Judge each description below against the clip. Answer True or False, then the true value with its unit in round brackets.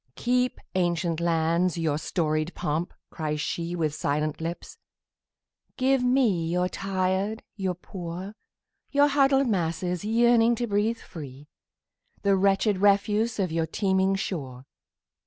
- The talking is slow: True (110 wpm)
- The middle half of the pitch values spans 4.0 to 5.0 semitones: True (4.6 semitones)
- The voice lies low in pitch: False (185 Hz)